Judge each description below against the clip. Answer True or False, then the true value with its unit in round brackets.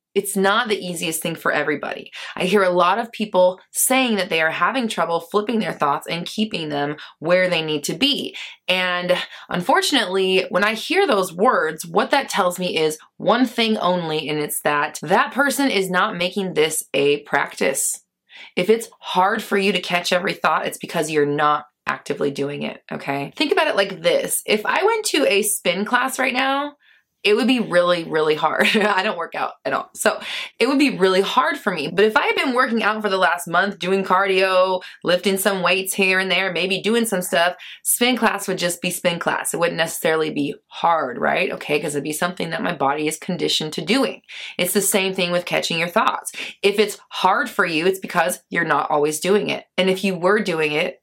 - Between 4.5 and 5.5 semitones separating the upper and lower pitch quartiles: False (4.0 semitones)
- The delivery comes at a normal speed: False (215 wpm)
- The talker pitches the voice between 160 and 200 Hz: True (185 Hz)